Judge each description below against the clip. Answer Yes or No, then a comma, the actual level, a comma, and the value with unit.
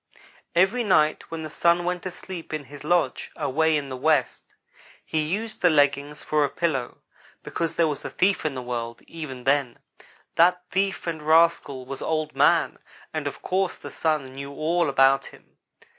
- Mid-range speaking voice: Yes, medium, 155 Hz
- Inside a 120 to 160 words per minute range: No, average, 180 wpm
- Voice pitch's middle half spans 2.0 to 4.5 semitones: Yes, average, 3.6 semitones